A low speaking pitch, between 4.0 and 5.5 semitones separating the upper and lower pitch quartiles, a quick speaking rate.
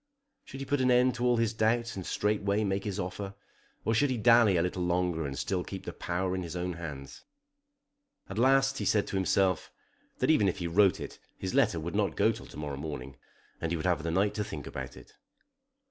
Yes: very low, 95 Hz; average, 4.5 semitones; fast, 230 wpm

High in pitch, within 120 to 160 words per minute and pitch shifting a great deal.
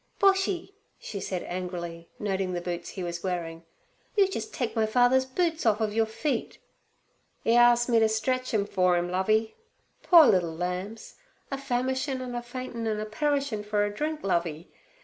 No: high, 220 Hz; average, 180 wpm; wide, 5.9 semitones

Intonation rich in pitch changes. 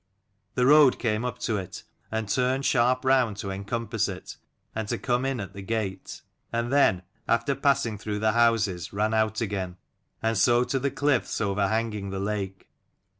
No: average, 3.8 semitones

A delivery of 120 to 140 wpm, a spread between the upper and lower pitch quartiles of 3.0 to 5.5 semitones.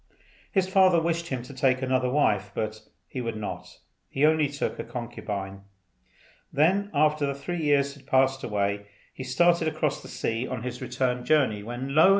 No: average, 175 wpm; average, 4.2 semitones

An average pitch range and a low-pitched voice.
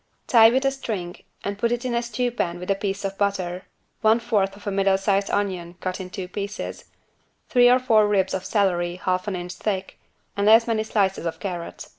No: average, 3.2 semitones; high, 200 Hz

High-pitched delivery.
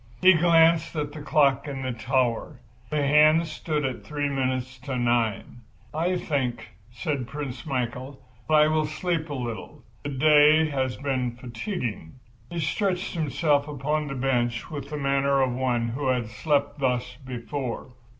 No: medium, 140 Hz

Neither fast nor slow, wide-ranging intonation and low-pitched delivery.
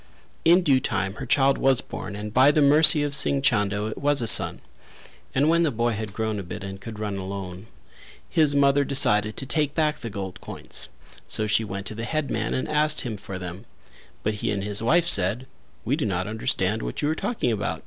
No: fast, 220 wpm; wide, 5.7 semitones; low, 115 Hz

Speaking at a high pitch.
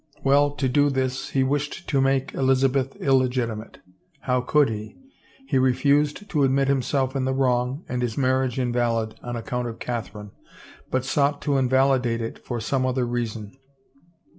No: low, 130 Hz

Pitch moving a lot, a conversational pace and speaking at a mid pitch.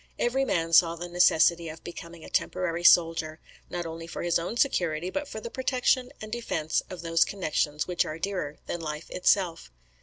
No: narrow, 2.6 semitones; average, 185 wpm; medium, 170 Hz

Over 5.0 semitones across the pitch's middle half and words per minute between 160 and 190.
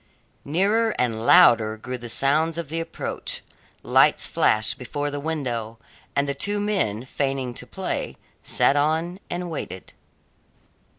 No: wide, 5.4 semitones; slow, 135 wpm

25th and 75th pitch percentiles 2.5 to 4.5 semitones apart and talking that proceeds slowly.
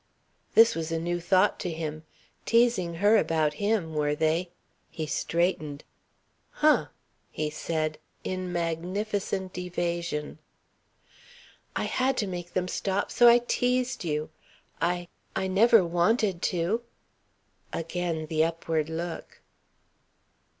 Yes: average, 3.7 semitones; slow, 115 wpm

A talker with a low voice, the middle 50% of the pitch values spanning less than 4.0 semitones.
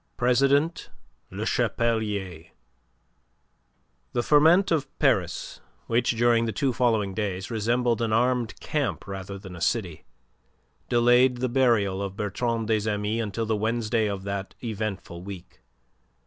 Yes: low, 110 Hz; average, 3.5 semitones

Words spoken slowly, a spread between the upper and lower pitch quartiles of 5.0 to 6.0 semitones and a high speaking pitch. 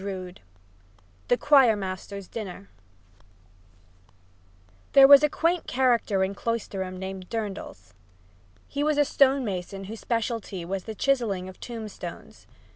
Yes: slow, 120 wpm; wide, 5.4 semitones; high, 215 Hz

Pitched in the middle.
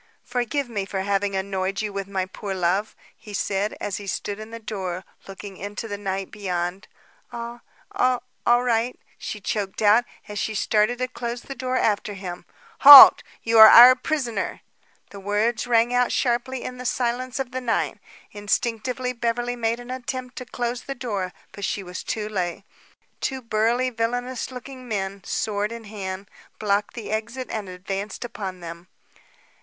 No: high, 220 Hz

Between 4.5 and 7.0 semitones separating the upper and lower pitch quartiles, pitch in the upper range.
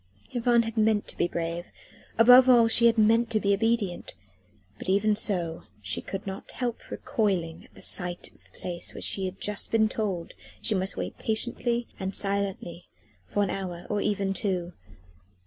No: average, 3.7 semitones; high, 200 Hz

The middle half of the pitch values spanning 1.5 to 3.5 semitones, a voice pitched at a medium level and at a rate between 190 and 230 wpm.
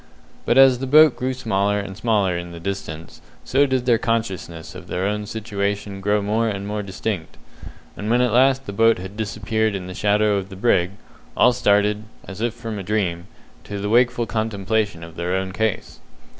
No: average, 2.9 semitones; low, 105 Hz; average, 195 wpm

